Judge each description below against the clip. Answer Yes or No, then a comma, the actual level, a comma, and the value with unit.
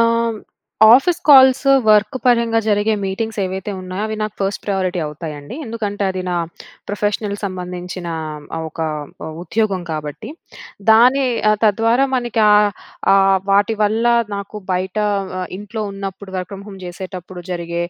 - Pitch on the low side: No, high, 200 Hz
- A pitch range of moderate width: Yes, average, 3.3 semitones